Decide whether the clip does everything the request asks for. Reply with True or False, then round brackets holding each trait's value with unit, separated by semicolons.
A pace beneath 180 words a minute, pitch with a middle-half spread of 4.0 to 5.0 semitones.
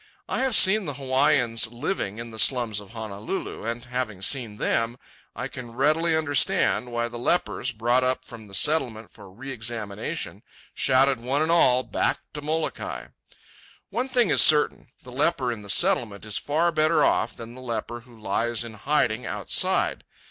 True (170 wpm; 4.4 semitones)